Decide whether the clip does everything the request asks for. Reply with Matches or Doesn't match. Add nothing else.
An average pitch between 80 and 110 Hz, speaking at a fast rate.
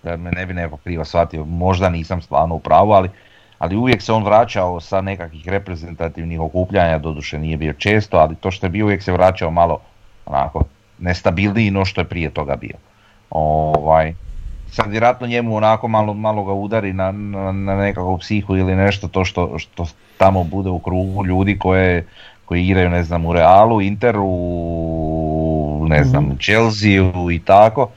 Matches